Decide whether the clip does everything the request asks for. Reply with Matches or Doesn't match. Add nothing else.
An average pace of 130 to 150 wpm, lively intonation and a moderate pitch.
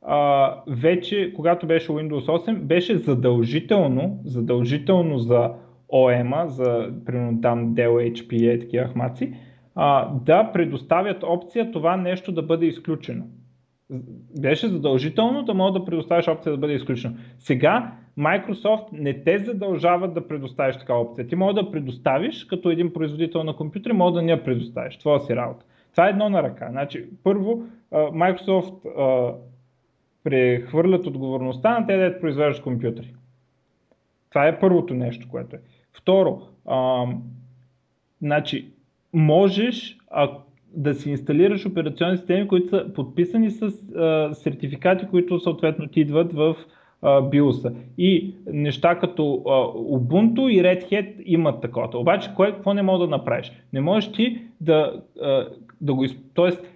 Matches